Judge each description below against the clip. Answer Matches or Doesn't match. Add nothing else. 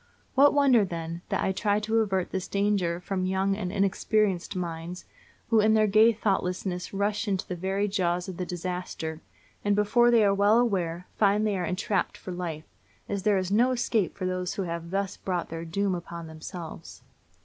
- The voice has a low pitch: Doesn't match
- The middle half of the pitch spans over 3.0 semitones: Doesn't match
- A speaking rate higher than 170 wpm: Matches